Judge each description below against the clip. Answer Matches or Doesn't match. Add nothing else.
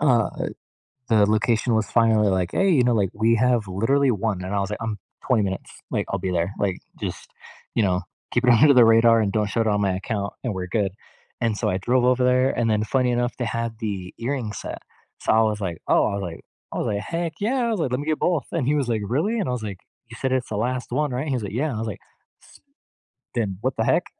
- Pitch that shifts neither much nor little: Matches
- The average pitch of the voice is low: Matches